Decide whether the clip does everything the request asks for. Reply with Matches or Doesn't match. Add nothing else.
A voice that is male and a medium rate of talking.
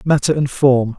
Matches